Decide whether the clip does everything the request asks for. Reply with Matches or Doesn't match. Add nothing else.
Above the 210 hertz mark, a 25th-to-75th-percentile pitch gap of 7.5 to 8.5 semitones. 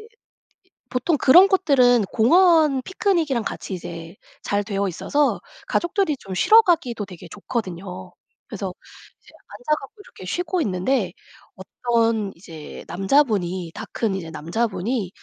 Matches